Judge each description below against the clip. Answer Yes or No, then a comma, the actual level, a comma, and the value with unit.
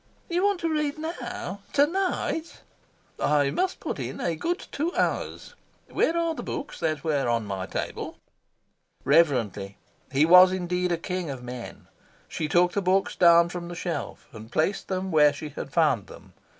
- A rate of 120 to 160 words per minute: No, average, 175 wpm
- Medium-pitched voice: Yes, medium, 175 Hz